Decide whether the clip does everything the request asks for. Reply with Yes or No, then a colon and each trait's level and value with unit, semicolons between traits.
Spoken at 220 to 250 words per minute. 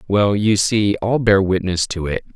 No: fast, 205 wpm